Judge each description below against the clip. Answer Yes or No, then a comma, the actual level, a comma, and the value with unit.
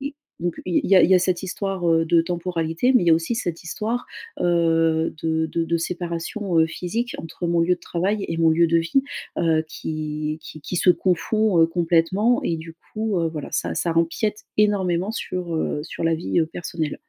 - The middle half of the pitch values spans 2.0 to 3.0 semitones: Yes, narrow, 2.4 semitones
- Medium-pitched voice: Yes, medium, 170 Hz